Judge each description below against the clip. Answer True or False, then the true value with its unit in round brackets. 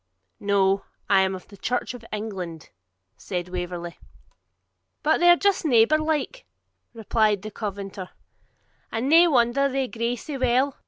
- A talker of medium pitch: False (225 Hz)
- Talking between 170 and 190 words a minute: False (140 wpm)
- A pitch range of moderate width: False (5.9 semitones)